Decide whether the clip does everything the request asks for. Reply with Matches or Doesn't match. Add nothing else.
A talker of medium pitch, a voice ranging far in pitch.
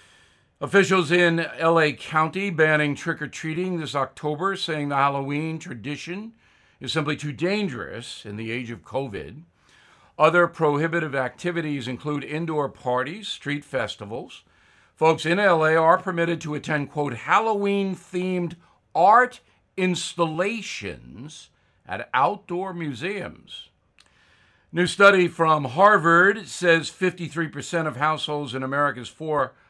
Doesn't match